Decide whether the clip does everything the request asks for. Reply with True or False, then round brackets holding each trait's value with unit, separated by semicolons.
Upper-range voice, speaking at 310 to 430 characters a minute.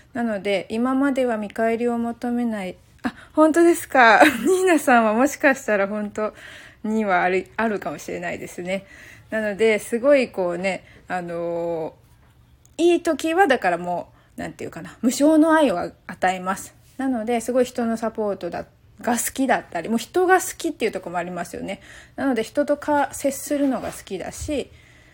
True (230 Hz; 340 characters per minute)